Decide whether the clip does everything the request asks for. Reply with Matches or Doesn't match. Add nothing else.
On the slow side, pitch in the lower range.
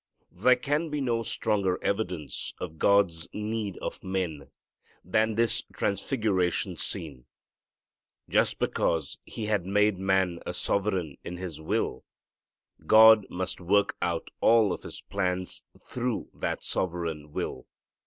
Matches